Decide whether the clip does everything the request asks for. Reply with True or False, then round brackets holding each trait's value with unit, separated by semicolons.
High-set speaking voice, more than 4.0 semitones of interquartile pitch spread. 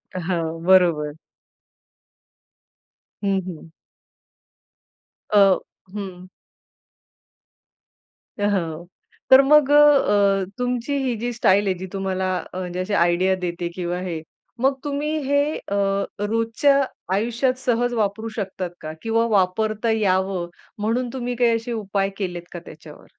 True (200 Hz; 4.7 semitones)